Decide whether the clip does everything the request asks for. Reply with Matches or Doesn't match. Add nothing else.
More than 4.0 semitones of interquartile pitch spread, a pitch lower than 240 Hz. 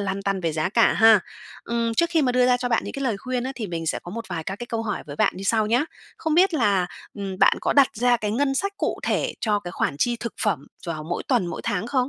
Matches